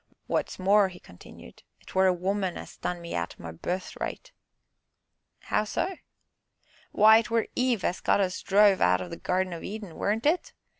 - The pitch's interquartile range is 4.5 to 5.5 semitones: No, average, 3.3 semitones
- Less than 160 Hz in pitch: No, high, 190 Hz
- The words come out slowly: No, average, 170 wpm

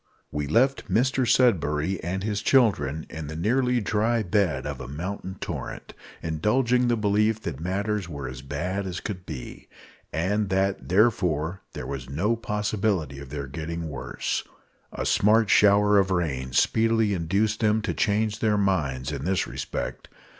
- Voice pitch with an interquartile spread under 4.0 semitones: No, wide, 5.5 semitones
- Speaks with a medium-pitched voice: No, very low, 95 Hz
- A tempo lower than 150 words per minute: No, average, 155 wpm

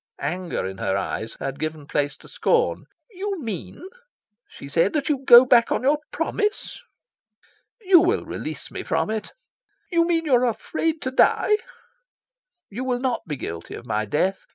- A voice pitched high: Yes, high, 245 Hz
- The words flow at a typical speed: Yes, average, 170 wpm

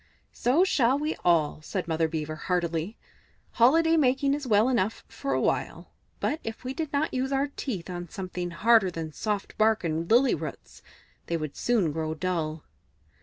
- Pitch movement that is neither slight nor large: No, wide, 7.8 semitones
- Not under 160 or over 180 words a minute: Yes, average, 170 wpm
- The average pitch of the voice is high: Yes, high, 205 Hz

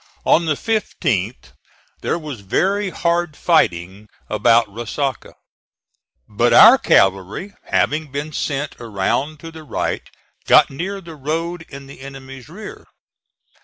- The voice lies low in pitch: No, medium, 145 Hz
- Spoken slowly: Yes, slow, 125 wpm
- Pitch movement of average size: No, wide, 6.3 semitones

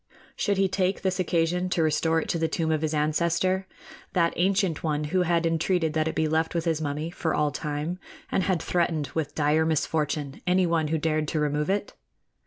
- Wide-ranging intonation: No, narrow, 2.6 semitones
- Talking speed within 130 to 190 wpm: No, average, 200 wpm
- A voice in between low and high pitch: Yes, medium, 160 Hz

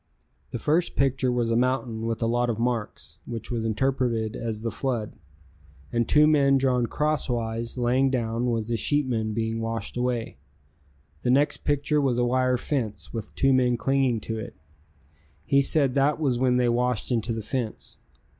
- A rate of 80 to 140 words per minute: No, average, 175 wpm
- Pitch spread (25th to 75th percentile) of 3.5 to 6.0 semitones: No, average, 2.7 semitones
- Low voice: Yes, low, 120 Hz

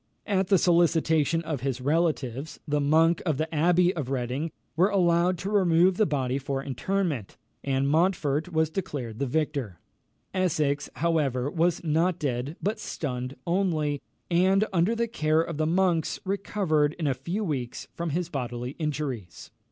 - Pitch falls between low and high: Yes, medium, 160 Hz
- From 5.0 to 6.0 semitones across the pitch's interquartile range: No, average, 4.1 semitones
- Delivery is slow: No, average, 155 wpm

